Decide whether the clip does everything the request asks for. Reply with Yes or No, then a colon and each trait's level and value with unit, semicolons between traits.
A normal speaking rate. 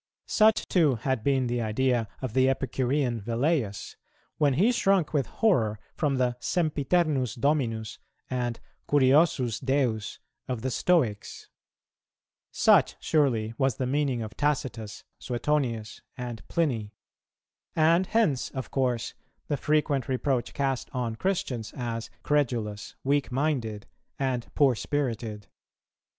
No: slow, 120 wpm